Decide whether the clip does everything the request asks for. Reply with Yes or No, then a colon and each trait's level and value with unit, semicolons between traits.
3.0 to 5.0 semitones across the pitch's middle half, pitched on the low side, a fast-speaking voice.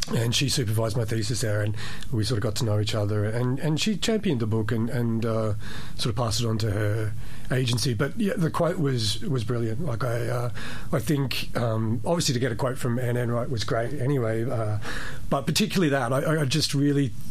Yes: average, 3.7 semitones; low, 120 Hz; fast, 220 wpm